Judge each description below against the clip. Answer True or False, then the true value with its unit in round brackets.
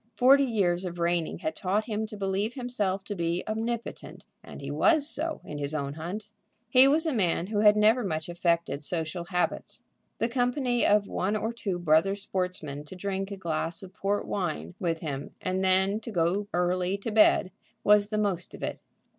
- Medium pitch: False (195 Hz)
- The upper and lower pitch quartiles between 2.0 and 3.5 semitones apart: False (3.9 semitones)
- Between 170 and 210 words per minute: True (190 wpm)